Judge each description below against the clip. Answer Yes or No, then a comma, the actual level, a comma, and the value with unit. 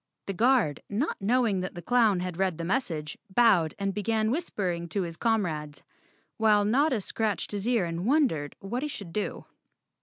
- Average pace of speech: Yes, average, 175 wpm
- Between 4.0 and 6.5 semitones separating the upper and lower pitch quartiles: Yes, average, 5.0 semitones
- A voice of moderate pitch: No, high, 205 Hz